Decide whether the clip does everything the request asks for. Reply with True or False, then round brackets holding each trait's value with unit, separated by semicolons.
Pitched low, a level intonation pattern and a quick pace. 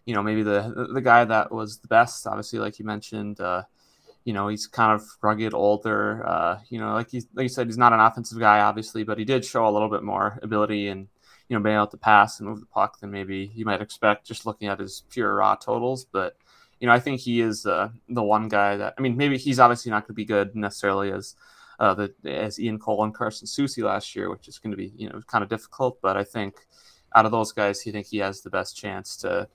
True (110 Hz; 2.0 semitones; 260 wpm)